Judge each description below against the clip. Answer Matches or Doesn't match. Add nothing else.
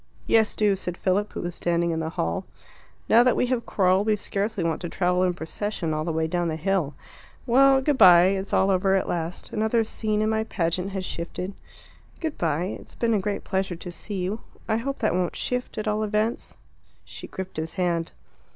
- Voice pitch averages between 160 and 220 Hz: Matches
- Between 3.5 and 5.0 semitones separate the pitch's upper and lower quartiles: Matches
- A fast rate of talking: Matches